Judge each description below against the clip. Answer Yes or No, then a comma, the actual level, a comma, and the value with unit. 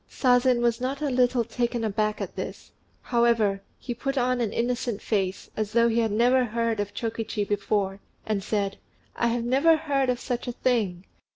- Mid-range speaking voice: No, high, 235 Hz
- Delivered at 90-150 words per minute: No, average, 180 wpm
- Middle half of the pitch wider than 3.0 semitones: No, average, 2.7 semitones